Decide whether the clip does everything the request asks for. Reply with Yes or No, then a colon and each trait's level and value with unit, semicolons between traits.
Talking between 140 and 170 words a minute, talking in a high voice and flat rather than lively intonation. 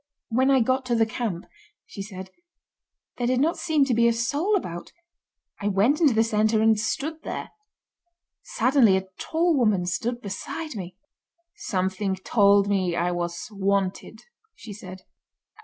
No: average, 155 wpm; high, 215 Hz; average, 5.2 semitones